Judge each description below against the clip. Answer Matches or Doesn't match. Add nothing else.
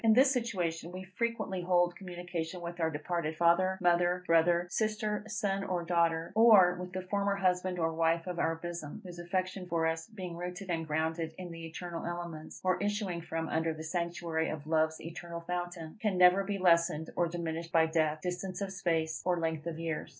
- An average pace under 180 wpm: Doesn't match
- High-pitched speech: Doesn't match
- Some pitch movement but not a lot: Doesn't match